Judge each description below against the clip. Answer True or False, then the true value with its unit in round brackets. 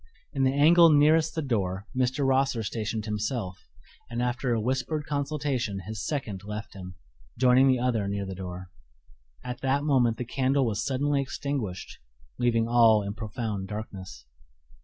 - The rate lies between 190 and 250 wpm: False (155 wpm)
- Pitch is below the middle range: True (120 Hz)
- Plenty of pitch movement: False (4.5 semitones)